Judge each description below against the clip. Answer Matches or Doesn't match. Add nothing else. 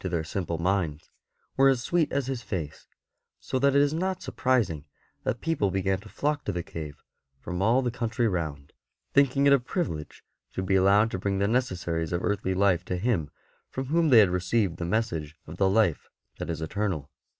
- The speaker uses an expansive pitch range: Matches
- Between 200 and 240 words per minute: Matches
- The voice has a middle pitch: Doesn't match